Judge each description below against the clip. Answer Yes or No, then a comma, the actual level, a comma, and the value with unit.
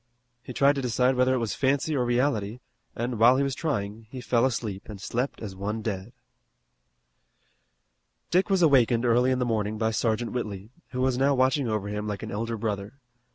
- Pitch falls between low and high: No, low, 120 Hz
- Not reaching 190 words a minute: No, average, 195 wpm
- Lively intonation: No, average, 3.4 semitones